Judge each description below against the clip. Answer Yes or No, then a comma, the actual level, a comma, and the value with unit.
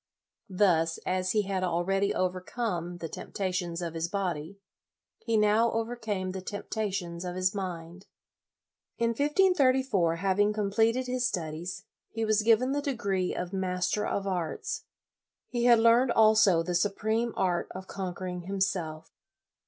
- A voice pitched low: No, high, 195 Hz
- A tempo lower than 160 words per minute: Yes, average, 140 wpm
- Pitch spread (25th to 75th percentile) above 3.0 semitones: Yes, average, 3.8 semitones